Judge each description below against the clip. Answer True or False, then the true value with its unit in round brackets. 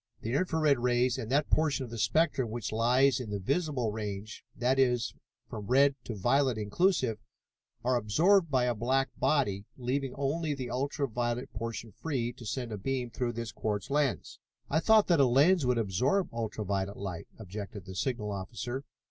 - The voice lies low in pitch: True (125 Hz)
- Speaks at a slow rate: False (180 wpm)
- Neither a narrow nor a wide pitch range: True (4.2 semitones)